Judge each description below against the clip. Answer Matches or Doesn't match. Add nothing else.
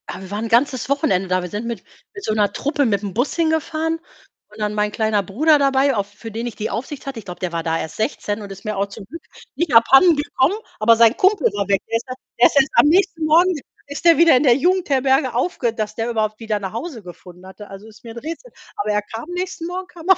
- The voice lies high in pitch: Matches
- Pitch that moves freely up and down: Matches